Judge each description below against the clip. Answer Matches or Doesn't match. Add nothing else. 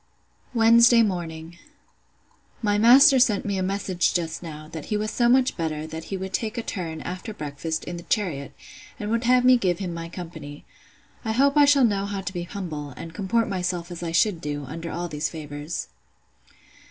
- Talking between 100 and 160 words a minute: Doesn't match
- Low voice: Doesn't match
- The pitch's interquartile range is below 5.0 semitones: Doesn't match